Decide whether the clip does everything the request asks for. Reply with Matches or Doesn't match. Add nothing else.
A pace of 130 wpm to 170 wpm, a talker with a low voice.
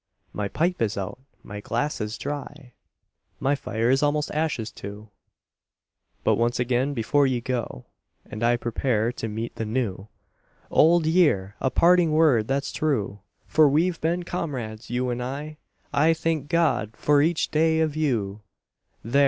Matches